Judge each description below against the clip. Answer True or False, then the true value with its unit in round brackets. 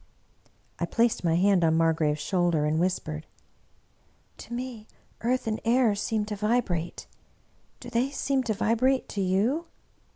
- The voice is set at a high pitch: True (210 Hz)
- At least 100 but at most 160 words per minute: True (150 wpm)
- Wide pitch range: True (5.8 semitones)